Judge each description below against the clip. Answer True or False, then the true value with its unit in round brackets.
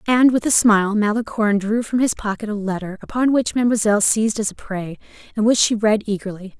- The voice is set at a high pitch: True (215 Hz)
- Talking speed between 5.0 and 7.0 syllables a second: True (6.2 syllables/s)